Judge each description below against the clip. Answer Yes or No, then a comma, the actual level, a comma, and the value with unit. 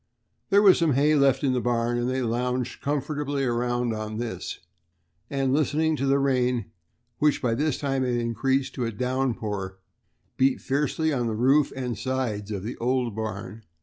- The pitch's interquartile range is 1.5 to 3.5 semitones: Yes, average, 3.1 semitones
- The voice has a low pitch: Yes, low, 125 Hz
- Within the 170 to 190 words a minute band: Yes, average, 180 wpm